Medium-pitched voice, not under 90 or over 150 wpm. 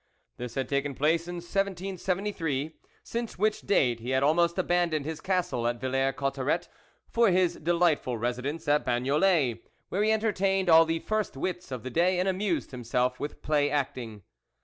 No: medium, 160 Hz; average, 165 wpm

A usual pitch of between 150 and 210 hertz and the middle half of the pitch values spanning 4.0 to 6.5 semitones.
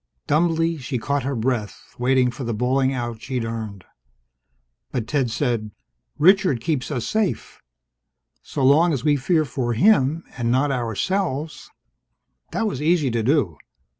No: low, 135 Hz; average, 4.6 semitones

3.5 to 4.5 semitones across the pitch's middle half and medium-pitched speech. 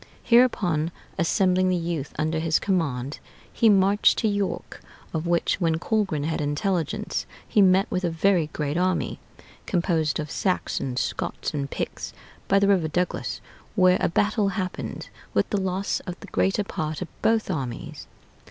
Yes: average, 3.8 semitones; medium, 180 Hz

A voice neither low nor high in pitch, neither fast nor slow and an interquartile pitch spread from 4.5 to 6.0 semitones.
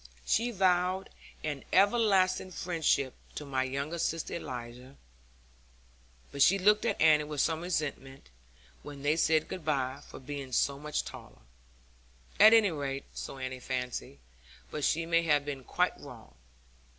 Yes: medium, 150 Hz; average, 145 wpm; average, 4.8 semitones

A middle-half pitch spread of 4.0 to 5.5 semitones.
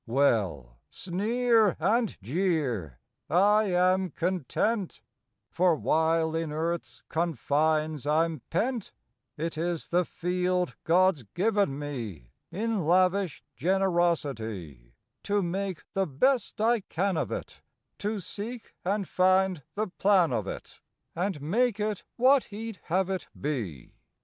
Yes: average, 4.7 semitones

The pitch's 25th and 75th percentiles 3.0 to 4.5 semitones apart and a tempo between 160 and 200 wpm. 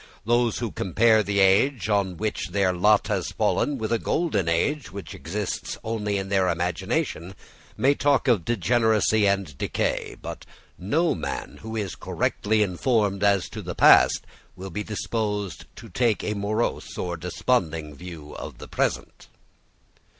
No: average, 3.5 semitones; average, 150 wpm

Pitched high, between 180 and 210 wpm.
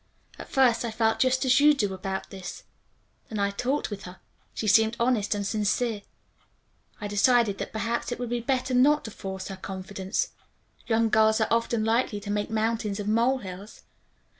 Yes: high, 220 Hz; average, 185 wpm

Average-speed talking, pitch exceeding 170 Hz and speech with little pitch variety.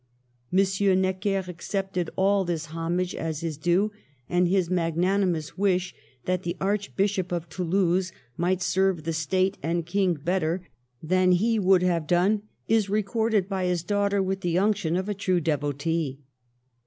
Yes: average, 150 wpm; medium, 185 Hz; narrow, 2.3 semitones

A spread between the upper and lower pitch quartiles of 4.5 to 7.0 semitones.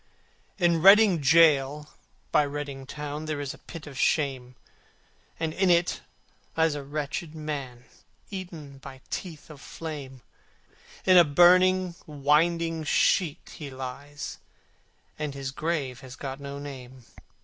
No: average, 3.2 semitones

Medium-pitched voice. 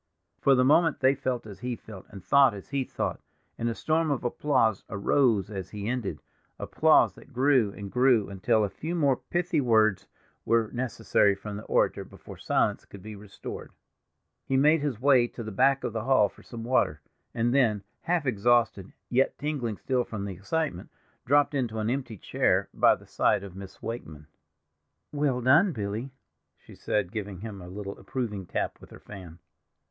No: low, 115 Hz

